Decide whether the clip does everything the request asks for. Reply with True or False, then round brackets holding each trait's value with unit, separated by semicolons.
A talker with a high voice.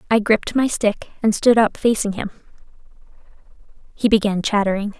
True (215 Hz)